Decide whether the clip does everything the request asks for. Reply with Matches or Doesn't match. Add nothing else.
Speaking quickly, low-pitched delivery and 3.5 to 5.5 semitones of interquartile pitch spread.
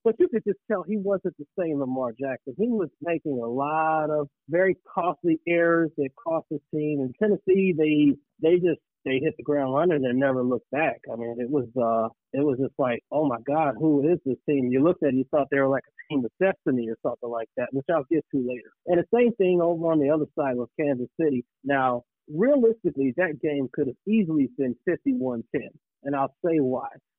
Doesn't match